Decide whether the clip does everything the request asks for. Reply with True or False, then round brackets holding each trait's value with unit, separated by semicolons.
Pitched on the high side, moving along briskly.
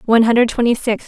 True (235 Hz; 225 wpm)